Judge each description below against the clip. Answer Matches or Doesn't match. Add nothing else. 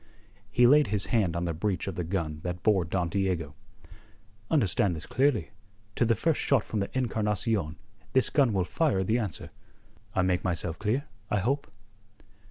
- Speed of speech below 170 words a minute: Doesn't match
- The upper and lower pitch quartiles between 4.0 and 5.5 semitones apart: Matches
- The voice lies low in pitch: Matches